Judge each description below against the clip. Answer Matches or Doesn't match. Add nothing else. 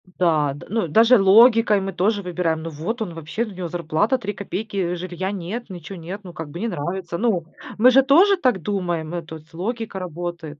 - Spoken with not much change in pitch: Doesn't match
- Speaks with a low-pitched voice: Doesn't match